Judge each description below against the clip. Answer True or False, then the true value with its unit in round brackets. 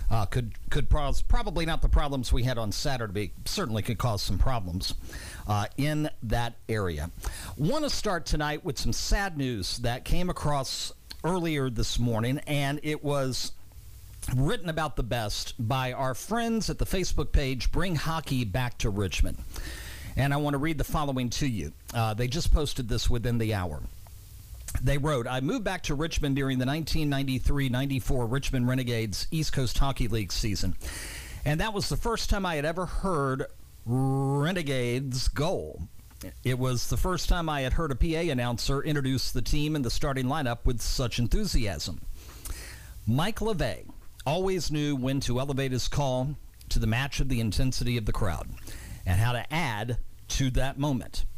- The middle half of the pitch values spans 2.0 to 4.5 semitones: False (5.3 semitones)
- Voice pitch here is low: True (130 Hz)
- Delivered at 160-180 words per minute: True (170 wpm)